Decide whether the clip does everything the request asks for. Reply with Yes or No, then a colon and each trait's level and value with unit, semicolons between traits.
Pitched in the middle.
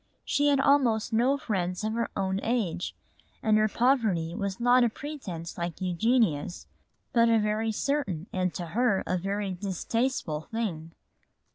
No: high, 215 Hz